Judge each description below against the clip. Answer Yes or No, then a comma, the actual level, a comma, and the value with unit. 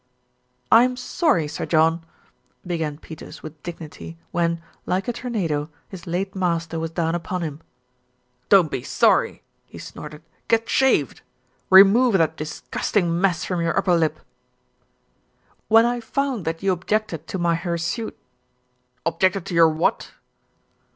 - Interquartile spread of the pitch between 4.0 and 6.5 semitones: No, average, 3.3 semitones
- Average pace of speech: Yes, average, 145 wpm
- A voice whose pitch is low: No, medium, 170 Hz